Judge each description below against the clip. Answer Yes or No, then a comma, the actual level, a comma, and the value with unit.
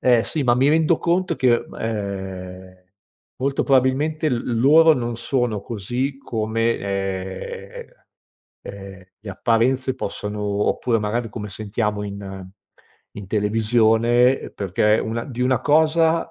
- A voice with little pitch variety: No, average, 4.3 semitones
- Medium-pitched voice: No, low, 115 Hz